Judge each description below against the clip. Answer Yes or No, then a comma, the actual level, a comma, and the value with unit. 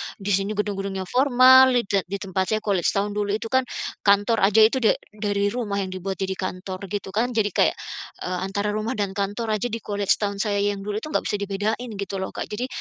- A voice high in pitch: Yes, high, 205 Hz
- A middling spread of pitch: No, narrow, 2.0 semitones